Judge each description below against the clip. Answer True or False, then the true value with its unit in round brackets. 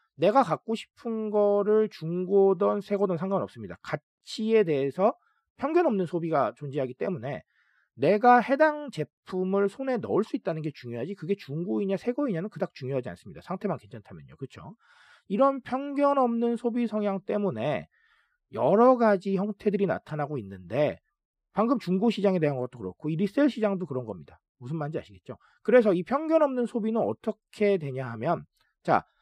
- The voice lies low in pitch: False (200 Hz)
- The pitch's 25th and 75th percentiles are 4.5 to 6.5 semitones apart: False (7.2 semitones)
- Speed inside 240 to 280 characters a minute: False (355 characters per minute)